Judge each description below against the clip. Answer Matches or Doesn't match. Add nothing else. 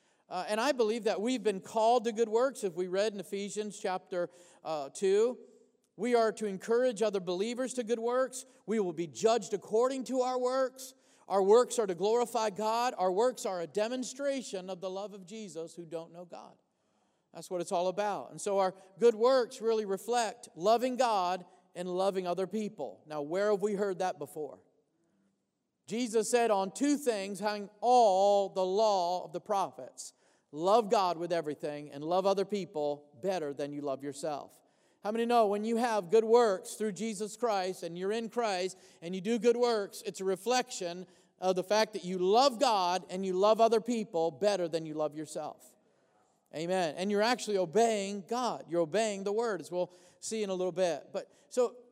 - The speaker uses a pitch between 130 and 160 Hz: Doesn't match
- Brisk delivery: Doesn't match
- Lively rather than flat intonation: Doesn't match